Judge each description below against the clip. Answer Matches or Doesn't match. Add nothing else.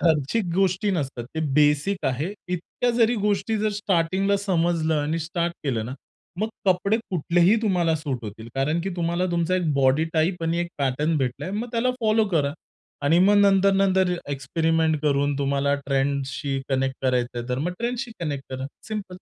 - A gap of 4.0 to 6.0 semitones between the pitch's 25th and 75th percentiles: Matches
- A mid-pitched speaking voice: Matches